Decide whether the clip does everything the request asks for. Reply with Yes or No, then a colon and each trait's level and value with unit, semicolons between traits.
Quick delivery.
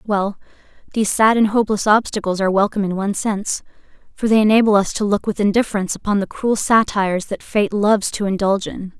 No: average, 195 wpm